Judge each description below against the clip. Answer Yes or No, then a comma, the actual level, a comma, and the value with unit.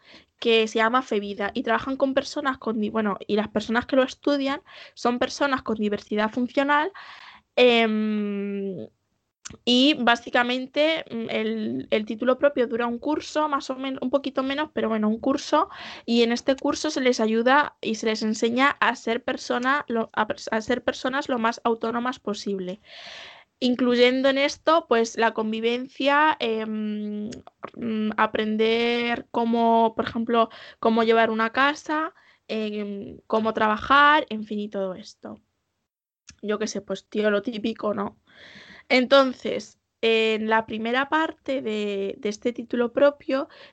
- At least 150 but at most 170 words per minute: No, average, 140 wpm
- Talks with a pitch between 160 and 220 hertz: No, high, 235 Hz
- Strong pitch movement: No, average, 3.7 semitones